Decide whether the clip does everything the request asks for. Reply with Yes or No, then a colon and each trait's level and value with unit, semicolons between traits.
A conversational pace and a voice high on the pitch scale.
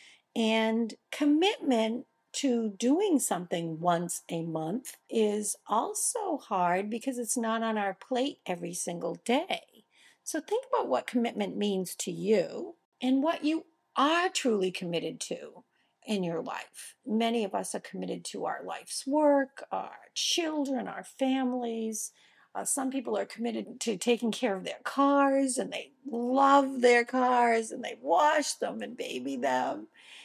Yes: average, 145 wpm; high, 245 Hz